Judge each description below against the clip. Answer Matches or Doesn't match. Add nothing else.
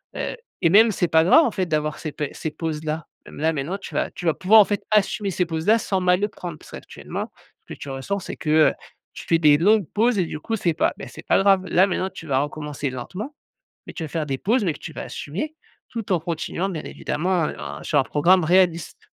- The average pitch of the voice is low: Doesn't match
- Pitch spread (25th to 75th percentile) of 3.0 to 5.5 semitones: Matches